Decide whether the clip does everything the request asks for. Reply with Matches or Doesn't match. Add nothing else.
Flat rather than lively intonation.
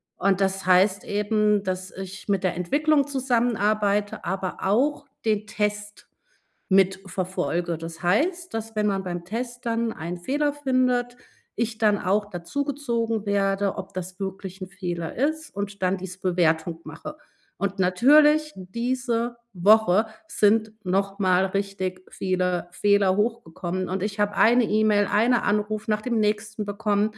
Doesn't match